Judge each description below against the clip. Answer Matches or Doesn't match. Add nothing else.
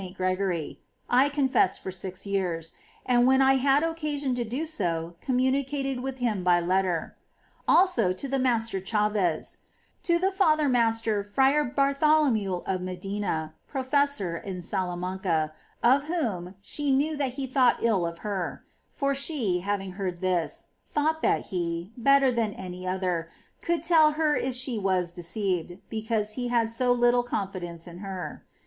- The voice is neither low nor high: Doesn't match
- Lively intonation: Matches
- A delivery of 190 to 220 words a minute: Doesn't match